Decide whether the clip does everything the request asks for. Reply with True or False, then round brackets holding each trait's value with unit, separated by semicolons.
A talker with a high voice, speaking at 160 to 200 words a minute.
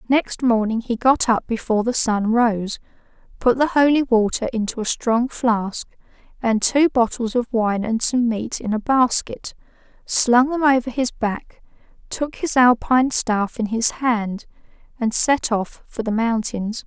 True (235 Hz; 165 wpm)